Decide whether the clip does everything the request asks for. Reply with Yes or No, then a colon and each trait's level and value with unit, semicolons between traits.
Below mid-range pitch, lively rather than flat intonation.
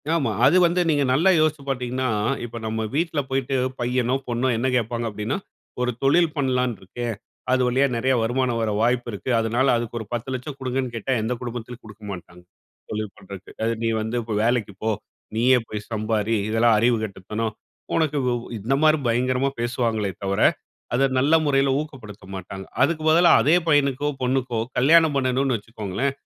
No: low, 125 Hz; average, 3.3 semitones